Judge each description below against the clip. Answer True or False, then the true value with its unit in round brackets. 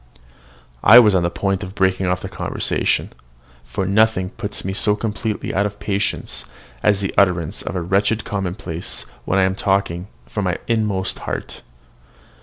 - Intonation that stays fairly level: True (2.0 semitones)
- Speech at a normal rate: True (165 wpm)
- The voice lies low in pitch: True (95 Hz)